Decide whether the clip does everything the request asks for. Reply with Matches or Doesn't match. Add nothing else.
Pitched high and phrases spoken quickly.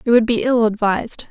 Matches